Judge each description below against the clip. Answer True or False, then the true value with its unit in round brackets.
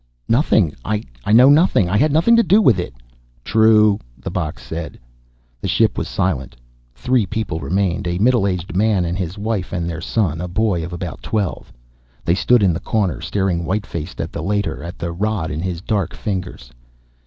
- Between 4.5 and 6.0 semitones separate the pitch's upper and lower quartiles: False (4.1 semitones)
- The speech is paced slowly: False (190 wpm)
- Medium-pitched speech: False (95 Hz)